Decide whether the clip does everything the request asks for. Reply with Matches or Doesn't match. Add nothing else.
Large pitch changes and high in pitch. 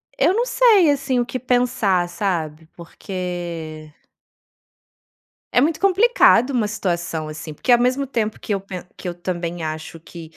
Matches